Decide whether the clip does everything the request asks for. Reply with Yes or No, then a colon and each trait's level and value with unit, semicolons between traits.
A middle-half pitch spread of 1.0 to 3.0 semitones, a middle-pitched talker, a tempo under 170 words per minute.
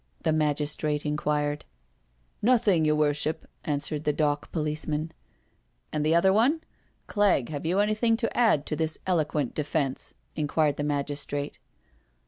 Yes: narrow, 2.5 semitones; medium, 150 Hz; average, 150 wpm